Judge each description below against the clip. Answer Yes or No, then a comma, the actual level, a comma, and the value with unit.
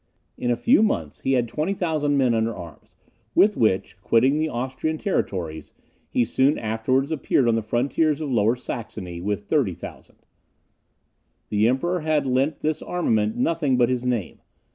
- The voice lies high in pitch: No, low, 125 Hz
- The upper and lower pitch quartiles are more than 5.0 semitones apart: Yes, wide, 5.4 semitones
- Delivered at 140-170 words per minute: Yes, average, 155 wpm